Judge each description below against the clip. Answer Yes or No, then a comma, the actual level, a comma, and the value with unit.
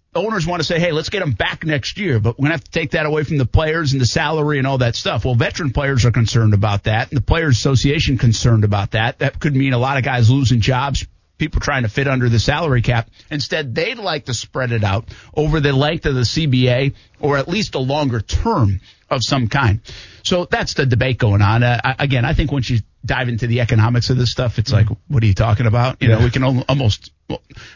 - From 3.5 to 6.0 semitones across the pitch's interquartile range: Yes, average, 3.8 semitones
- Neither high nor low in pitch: No, low, 125 Hz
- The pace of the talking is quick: Yes, fast, 250 wpm